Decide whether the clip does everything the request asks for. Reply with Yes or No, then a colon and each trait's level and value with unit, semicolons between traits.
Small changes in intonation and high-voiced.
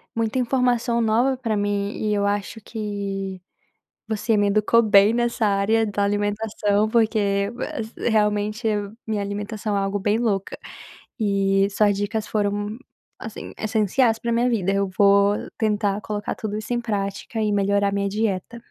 Yes: narrow, 1.8 semitones; high, 210 Hz